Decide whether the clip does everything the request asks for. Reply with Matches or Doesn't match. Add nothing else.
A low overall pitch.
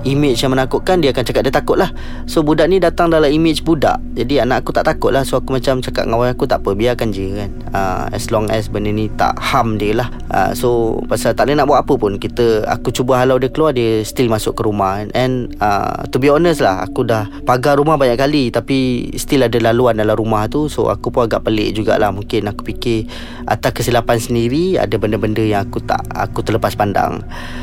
Matches